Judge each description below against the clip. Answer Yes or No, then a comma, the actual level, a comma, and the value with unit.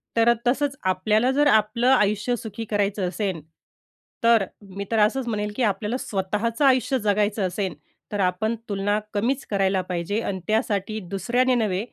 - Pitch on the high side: Yes, high, 210 Hz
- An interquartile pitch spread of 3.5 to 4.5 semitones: No, average, 3.0 semitones